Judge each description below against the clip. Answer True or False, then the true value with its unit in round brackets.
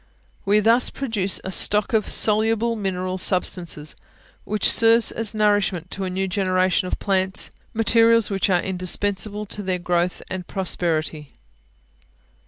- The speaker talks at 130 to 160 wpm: True (135 wpm)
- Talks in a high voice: True (195 Hz)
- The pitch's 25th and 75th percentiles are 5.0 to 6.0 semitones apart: False (2.6 semitones)